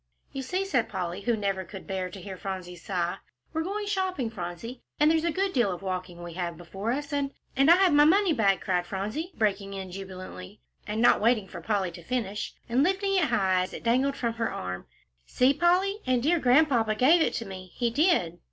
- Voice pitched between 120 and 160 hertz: No, high, 225 Hz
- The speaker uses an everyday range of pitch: No, wide, 7.8 semitones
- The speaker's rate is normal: No, fast, 220 wpm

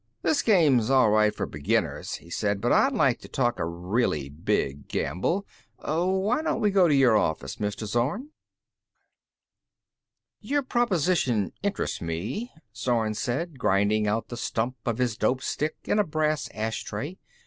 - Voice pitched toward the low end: Yes, low, 120 Hz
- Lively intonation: Yes, wide, 8.6 semitones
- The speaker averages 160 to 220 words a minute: No, average, 150 wpm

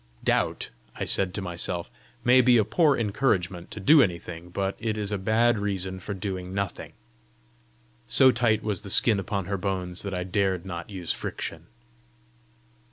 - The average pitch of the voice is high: No, low, 100 Hz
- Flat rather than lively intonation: No, average, 3.2 semitones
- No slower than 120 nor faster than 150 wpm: No, average, 165 wpm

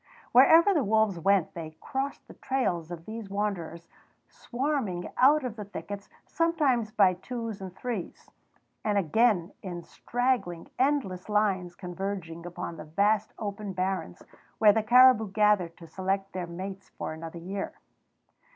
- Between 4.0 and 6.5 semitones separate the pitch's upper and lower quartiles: Yes, average, 4.5 semitones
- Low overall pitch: No, high, 200 Hz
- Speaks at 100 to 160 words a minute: Yes, average, 140 wpm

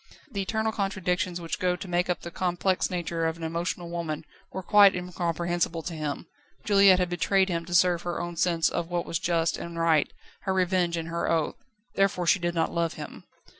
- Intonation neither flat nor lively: No, narrow, 1.6 semitones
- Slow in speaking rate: No, fast, 205 wpm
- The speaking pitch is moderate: Yes, medium, 175 Hz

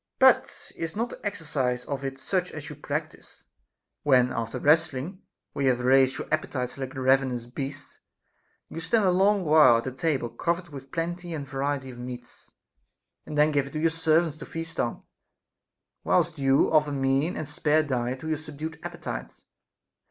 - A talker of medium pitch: Yes, medium, 145 Hz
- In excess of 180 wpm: No, average, 175 wpm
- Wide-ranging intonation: No, average, 3.5 semitones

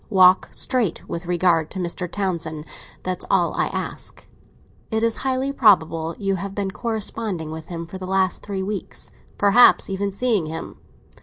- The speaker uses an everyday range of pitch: Yes, average, 3.6 semitones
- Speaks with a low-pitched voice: No, high, 190 Hz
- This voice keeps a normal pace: Yes, average, 155 wpm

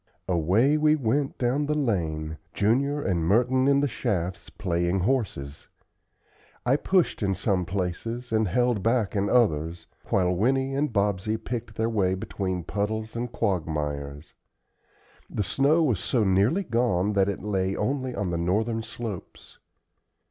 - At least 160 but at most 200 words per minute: No, average, 145 wpm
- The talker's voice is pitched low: Yes, low, 105 Hz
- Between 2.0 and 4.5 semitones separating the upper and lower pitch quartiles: No, average, 5.3 semitones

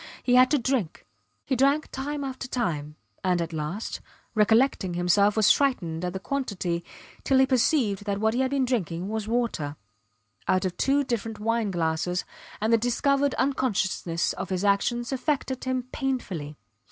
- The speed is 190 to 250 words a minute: No, average, 165 wpm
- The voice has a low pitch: No, high, 220 Hz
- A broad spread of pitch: Yes, wide, 6.4 semitones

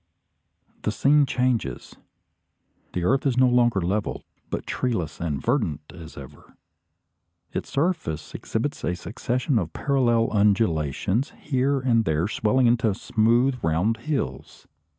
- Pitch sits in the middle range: No, low, 115 Hz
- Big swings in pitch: Yes, wide, 6.9 semitones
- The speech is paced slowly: Yes, slow, 125 wpm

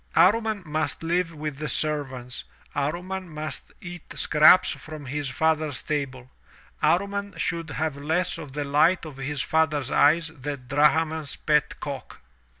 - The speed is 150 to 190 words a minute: No, average, 140 wpm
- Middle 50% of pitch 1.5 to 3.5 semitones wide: Yes, narrow, 2.5 semitones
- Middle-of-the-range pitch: Yes, medium, 155 Hz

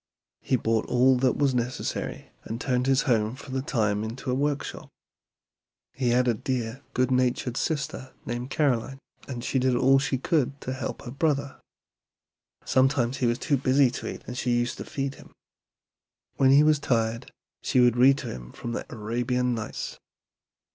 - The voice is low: Yes, low, 125 Hz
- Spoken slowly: No, average, 175 wpm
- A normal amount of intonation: No, narrow, 2.1 semitones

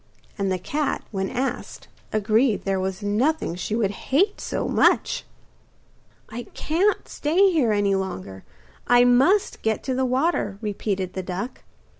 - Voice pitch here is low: No, high, 220 Hz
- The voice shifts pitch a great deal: Yes, wide, 5.8 semitones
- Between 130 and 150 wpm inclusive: Yes, average, 145 wpm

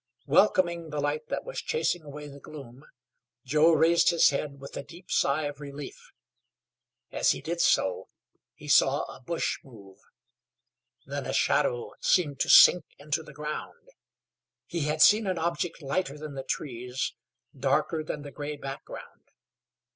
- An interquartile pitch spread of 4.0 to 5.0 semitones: No, average, 3.3 semitones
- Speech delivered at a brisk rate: No, average, 155 wpm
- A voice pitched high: No, medium, 150 Hz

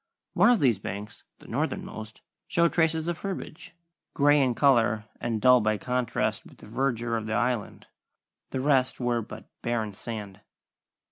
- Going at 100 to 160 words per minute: Yes, average, 155 wpm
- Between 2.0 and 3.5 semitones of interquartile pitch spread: No, average, 4.2 semitones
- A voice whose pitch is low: Yes, low, 120 Hz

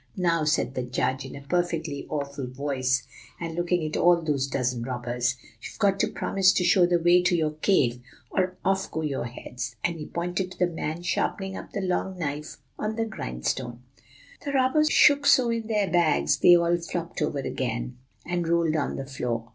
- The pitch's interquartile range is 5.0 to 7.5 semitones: Yes, average, 5.3 semitones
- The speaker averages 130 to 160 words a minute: No, average, 195 wpm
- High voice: No, medium, 165 Hz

